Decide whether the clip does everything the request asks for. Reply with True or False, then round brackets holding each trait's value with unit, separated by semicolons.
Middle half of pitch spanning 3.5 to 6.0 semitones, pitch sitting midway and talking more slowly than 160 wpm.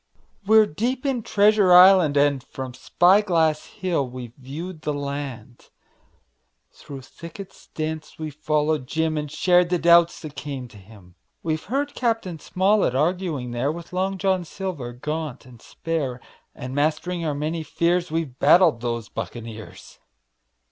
True (5.0 semitones; 155 Hz; 150 wpm)